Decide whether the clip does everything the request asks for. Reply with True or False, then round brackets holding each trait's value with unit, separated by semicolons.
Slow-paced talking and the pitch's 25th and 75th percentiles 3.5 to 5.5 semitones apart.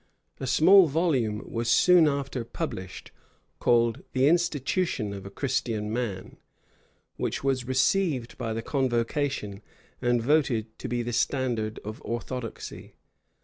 True (125 wpm; 3.8 semitones)